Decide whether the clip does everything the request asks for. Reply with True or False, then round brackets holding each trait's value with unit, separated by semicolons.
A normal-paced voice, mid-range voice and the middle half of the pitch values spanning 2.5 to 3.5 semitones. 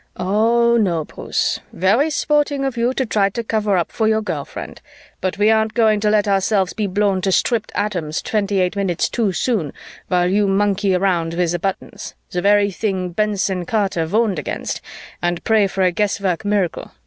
False (185 wpm; 200 Hz; 3.0 semitones)